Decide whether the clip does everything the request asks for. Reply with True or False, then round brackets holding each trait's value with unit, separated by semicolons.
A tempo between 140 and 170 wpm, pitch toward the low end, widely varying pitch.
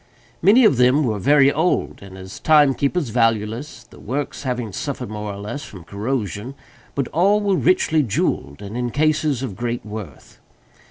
True (160 wpm; 125 Hz; 5.8 semitones)